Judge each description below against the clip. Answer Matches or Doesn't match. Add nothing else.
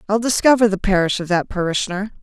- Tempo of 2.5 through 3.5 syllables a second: Doesn't match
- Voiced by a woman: Matches